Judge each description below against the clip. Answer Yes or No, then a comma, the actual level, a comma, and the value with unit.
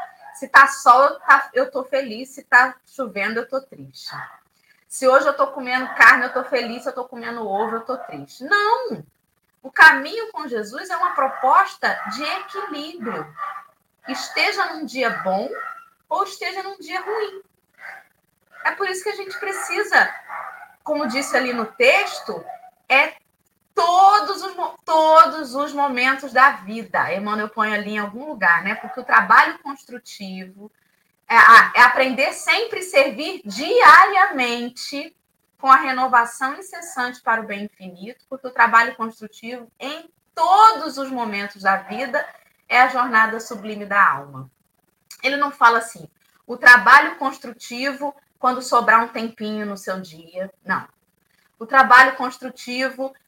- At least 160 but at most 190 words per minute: No, average, 145 wpm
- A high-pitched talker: Yes, very high, 265 Hz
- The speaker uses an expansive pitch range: Yes, wide, 5.7 semitones